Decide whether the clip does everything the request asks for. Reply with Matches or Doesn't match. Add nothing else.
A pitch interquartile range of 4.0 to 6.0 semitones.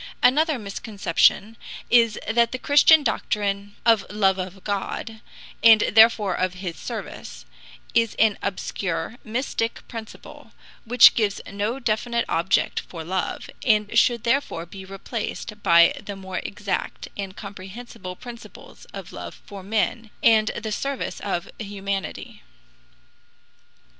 Doesn't match